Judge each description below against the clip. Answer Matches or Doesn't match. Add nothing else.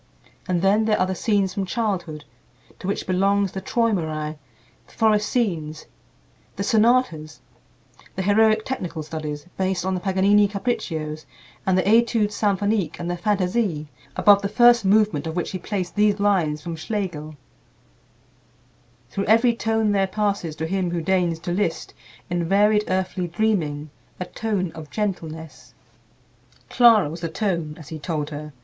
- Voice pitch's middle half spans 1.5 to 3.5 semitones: Doesn't match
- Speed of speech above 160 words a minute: Doesn't match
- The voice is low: Doesn't match